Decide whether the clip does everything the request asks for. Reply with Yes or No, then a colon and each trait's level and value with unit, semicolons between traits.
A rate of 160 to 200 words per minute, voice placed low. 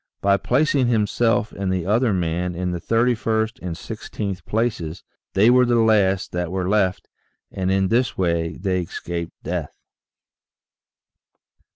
No: average, 140 wpm; low, 100 Hz